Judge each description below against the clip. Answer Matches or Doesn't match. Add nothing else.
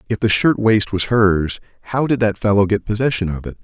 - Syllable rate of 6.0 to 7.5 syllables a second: Doesn't match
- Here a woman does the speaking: Doesn't match